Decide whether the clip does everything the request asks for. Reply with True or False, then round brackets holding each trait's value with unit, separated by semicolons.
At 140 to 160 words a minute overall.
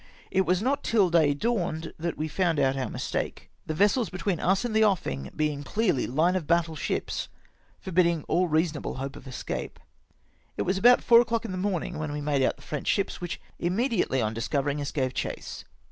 False (200 wpm)